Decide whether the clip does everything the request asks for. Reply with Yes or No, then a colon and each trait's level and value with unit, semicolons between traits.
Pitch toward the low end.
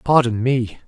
Yes: low, 120 Hz